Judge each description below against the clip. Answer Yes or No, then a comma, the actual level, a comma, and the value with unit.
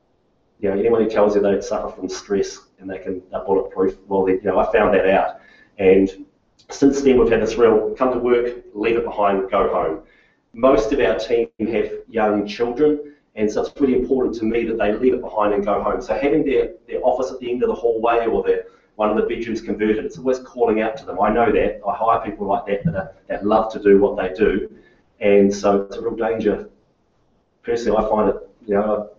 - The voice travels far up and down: Yes, wide, 5.7 semitones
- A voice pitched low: Yes, low, 110 Hz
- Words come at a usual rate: No, fast, 235 wpm